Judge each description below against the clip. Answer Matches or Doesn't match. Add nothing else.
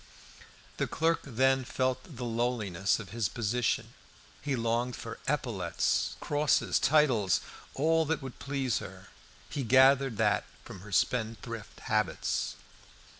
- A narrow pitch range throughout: Doesn't match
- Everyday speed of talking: Doesn't match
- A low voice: Matches